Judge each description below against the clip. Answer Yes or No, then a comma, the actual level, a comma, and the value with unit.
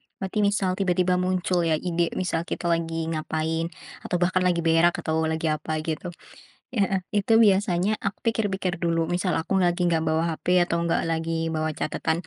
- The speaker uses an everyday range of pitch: No, narrow, 2.2 semitones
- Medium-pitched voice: Yes, medium, 175 Hz